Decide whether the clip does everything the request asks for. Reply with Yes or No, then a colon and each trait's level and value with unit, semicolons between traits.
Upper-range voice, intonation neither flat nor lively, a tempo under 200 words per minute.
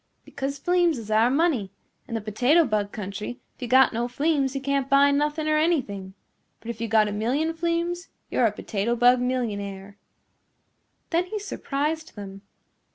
No: very high, 255 Hz; wide, 6.2 semitones; average, 170 wpm